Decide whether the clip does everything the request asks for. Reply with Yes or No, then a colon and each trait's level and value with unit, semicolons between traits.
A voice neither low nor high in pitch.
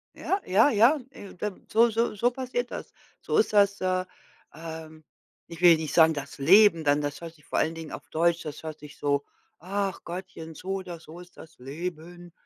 Yes: medium, 170 Hz